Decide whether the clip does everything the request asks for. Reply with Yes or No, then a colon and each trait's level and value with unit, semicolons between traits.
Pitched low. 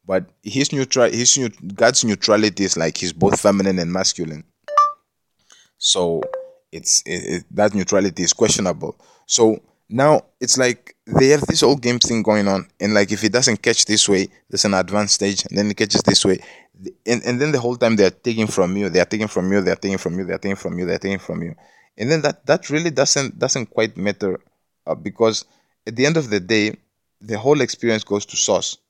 Yes: low, 105 Hz